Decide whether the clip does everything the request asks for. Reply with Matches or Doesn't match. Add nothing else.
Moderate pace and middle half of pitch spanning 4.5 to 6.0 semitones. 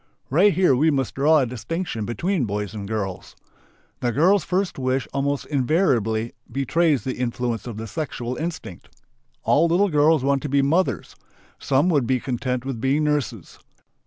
Matches